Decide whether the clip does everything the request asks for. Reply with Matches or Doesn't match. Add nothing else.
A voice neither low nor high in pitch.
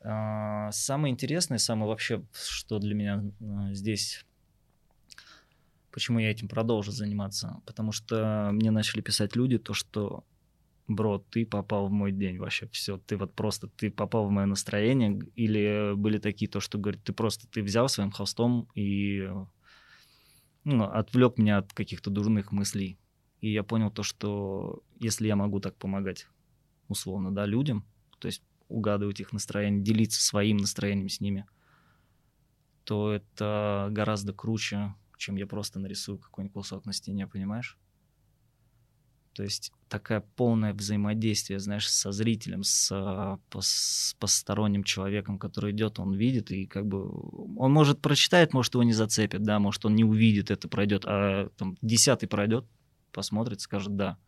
Doesn't match